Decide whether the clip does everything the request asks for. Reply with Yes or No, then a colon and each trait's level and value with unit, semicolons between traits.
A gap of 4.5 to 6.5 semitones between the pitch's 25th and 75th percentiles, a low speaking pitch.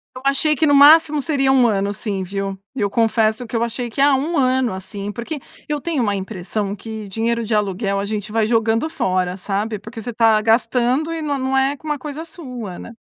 No: average, 5.0 semitones; high, 230 Hz